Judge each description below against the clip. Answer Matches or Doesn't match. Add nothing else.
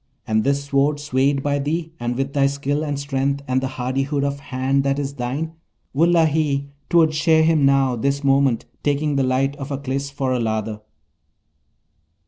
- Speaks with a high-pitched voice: Doesn't match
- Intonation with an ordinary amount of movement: Doesn't match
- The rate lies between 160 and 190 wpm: Matches